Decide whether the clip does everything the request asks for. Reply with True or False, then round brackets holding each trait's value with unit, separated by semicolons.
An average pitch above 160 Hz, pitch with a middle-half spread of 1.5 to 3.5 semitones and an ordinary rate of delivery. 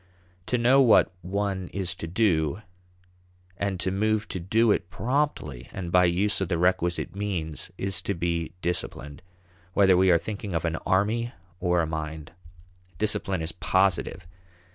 False (95 Hz; 3.2 semitones; 155 wpm)